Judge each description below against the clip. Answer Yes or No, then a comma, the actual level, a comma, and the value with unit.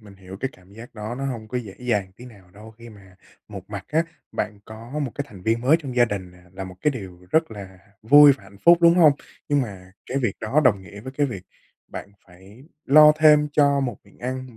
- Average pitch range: No, wide, 5.7 semitones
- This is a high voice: No, low, 115 Hz